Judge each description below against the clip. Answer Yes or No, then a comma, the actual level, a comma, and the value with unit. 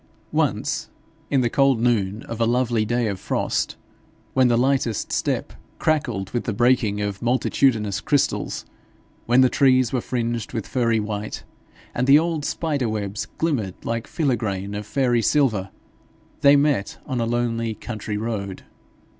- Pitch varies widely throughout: No, average, 3.5 semitones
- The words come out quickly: No, average, 150 wpm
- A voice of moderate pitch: No, low, 120 Hz